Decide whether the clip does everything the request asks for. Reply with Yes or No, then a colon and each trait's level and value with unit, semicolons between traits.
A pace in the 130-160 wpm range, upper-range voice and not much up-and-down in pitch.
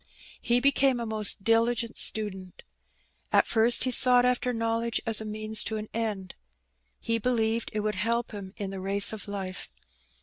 No: average, 175 wpm; high, 220 Hz; narrow, 2.1 semitones